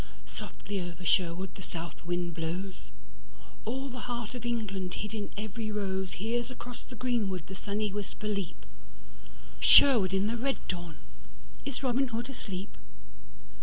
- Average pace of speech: No, slow, 130 wpm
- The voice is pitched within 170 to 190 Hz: No, high, 200 Hz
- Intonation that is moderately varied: Yes, average, 4.7 semitones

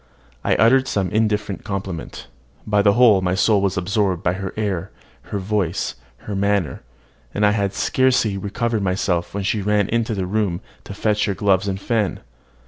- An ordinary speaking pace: Yes, average, 170 wpm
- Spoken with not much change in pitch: Yes, narrow, 1.9 semitones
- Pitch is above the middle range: No, low, 100 Hz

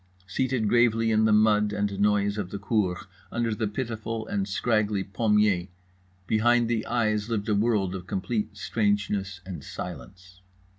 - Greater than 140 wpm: Yes, average, 150 wpm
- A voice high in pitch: No, low, 105 Hz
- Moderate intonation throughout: No, narrow, 2.3 semitones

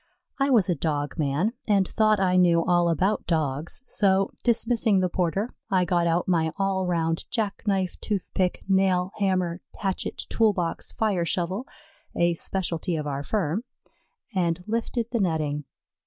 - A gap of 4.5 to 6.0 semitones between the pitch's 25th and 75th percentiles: No, average, 3.2 semitones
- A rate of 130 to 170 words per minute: Yes, average, 140 wpm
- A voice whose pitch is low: No, medium, 185 Hz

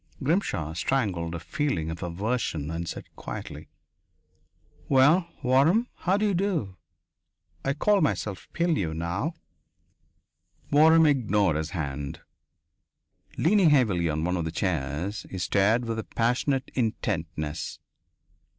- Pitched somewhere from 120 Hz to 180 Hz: No, low, 105 Hz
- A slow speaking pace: Yes, slow, 115 wpm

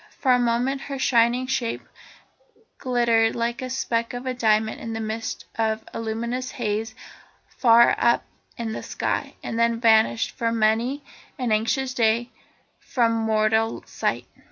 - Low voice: No, high, 230 Hz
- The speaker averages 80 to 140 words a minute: No, average, 150 wpm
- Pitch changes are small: Yes, narrow, 1.7 semitones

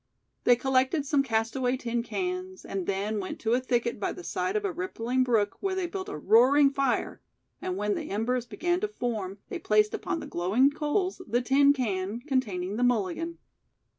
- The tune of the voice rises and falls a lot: Yes, wide, 6.9 semitones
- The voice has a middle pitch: No, very high, 255 Hz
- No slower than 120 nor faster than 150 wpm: No, average, 190 wpm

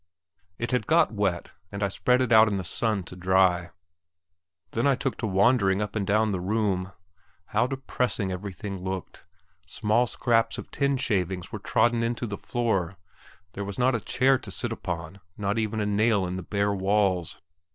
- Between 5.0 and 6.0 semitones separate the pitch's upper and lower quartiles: No, average, 3.7 semitones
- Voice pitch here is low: Yes, low, 105 Hz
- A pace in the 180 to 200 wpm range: Yes, average, 185 wpm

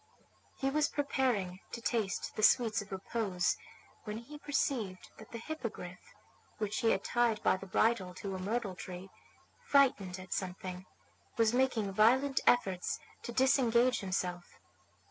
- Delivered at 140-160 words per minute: Yes, average, 145 wpm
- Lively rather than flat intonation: No, average, 4.5 semitones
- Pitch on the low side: No, high, 215 Hz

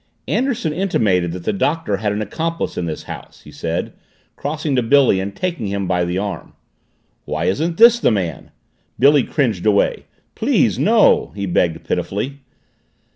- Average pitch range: No, wide, 8.7 semitones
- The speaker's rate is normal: Yes, average, 160 wpm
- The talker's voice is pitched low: Yes, low, 105 Hz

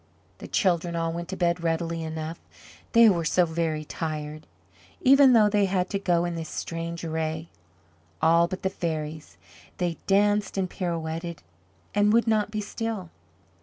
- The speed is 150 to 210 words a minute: Yes, average, 160 wpm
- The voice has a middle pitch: Yes, medium, 170 Hz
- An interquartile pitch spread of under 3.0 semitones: No, average, 3.4 semitones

